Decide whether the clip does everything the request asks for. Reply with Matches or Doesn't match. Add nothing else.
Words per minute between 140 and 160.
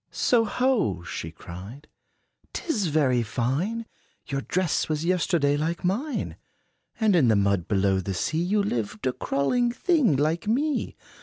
Matches